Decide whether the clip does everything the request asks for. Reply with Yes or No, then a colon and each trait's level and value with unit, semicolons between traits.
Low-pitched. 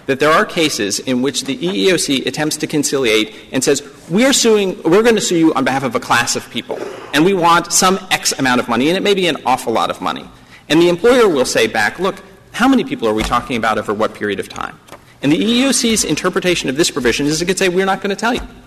No: medium, 170 Hz